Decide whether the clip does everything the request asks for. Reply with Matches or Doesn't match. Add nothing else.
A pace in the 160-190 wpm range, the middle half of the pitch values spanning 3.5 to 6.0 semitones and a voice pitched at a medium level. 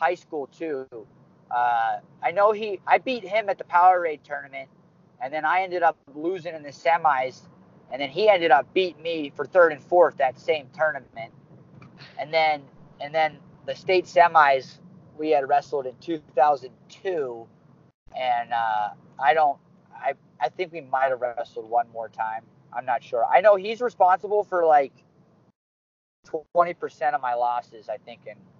Matches